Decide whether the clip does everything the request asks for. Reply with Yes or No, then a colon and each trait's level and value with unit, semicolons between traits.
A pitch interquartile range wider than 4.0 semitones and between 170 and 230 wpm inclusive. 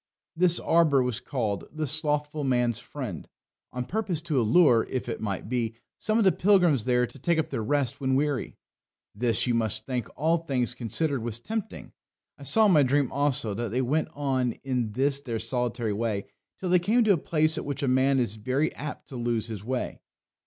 Yes: average, 4.4 semitones; average, 200 wpm